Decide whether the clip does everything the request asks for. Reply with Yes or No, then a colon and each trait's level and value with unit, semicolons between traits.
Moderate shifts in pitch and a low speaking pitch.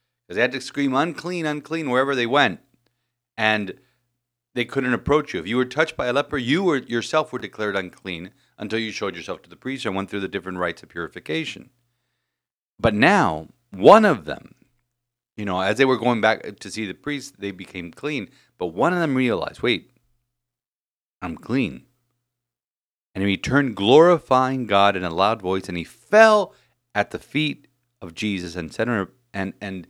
Yes: average, 4.9 semitones; low, 120 Hz